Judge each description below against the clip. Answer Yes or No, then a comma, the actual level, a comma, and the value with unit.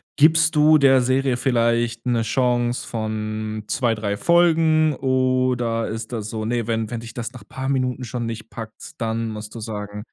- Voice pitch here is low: Yes, low, 120 Hz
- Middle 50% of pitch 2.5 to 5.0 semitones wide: Yes, average, 2.8 semitones